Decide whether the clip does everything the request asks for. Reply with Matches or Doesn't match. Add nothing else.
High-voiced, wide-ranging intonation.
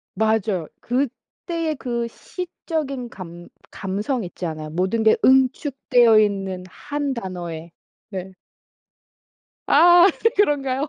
Matches